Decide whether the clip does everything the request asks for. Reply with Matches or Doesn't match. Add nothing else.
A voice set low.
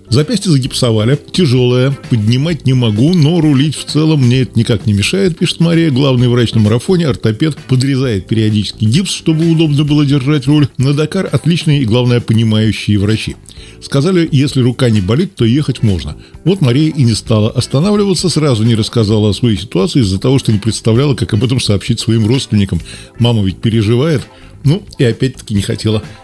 Matches